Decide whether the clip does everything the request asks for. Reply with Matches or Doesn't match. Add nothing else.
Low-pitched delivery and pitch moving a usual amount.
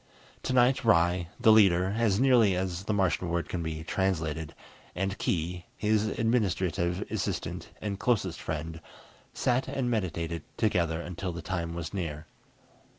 Matches